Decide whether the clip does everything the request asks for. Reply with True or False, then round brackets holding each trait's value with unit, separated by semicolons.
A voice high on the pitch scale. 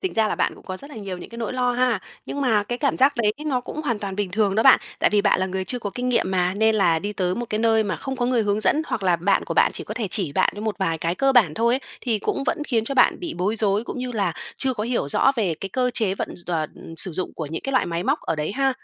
True (215 Hz)